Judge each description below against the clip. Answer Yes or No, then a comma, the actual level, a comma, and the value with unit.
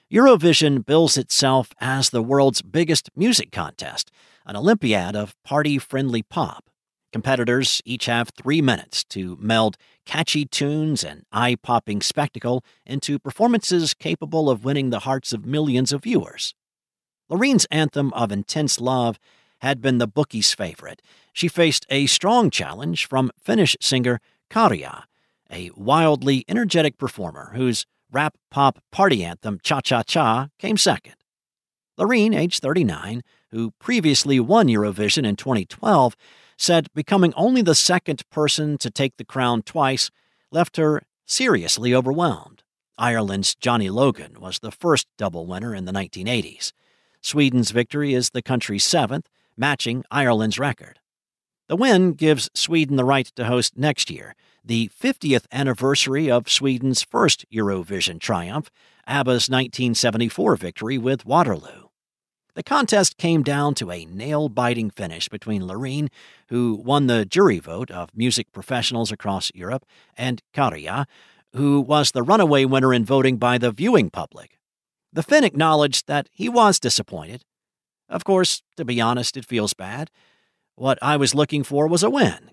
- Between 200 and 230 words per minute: No, average, 140 wpm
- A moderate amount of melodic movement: Yes, average, 4.3 semitones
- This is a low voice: Yes, low, 130 Hz